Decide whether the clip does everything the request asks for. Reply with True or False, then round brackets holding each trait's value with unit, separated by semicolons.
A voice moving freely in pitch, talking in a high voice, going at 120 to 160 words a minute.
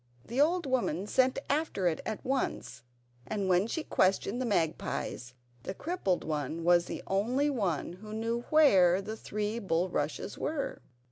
True (6.6 semitones; 210 Hz; 150 wpm)